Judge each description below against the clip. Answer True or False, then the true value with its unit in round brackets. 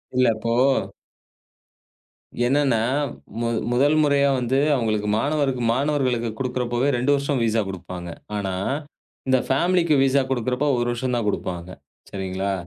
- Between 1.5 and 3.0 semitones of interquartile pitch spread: False (3.9 semitones)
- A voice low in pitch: True (125 Hz)